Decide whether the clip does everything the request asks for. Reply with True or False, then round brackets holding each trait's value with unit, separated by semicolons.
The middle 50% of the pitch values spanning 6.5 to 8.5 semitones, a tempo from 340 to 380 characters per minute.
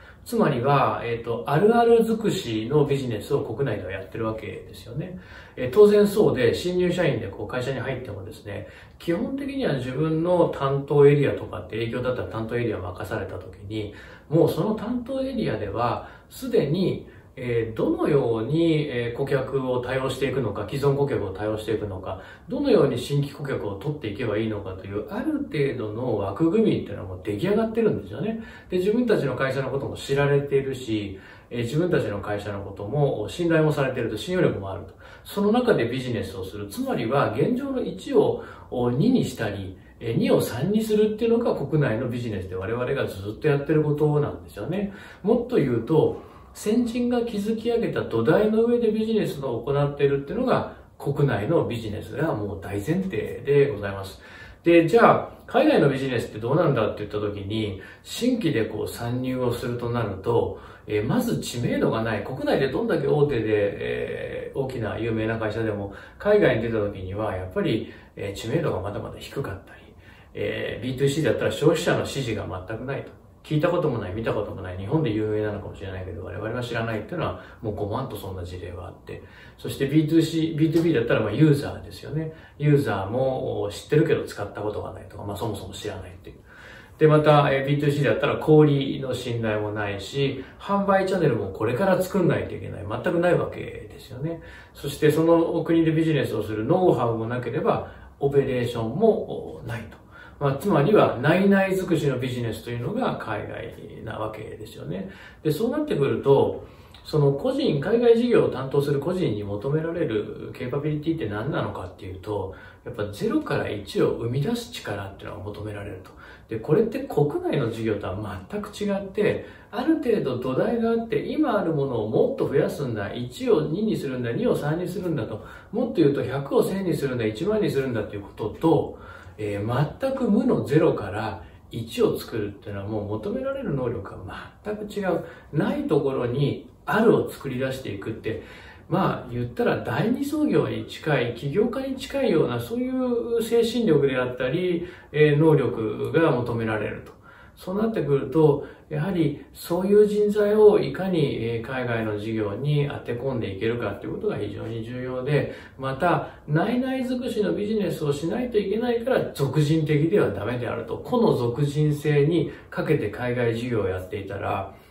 True (8.0 semitones; 375 characters per minute)